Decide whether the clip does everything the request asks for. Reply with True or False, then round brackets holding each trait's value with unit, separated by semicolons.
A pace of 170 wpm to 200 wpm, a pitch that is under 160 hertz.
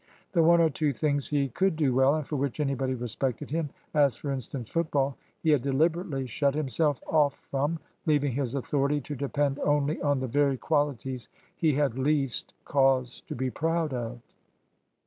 True (175 wpm; 140 Hz)